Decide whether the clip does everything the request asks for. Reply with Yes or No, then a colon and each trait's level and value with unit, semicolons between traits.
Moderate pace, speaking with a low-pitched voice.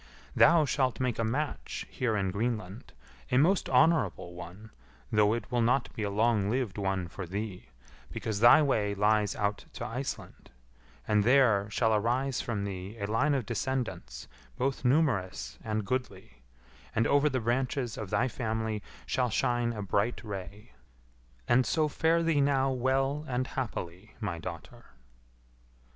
Yes: average, 155 wpm; low, 115 Hz